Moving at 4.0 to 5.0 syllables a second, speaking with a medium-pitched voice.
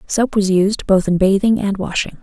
No: 4.8 syllables/s; high, 200 Hz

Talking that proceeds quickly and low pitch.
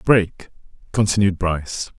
No: slow, 90 wpm; very low, 95 Hz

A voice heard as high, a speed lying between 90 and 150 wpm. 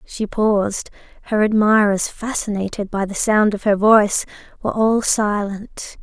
Yes: high, 210 Hz; average, 140 wpm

